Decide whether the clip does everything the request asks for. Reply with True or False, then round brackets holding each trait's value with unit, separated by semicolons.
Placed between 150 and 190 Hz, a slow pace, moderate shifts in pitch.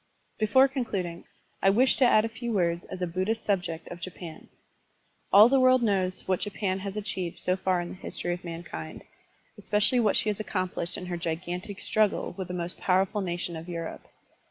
False (185 Hz; 205 wpm; 3.4 semitones)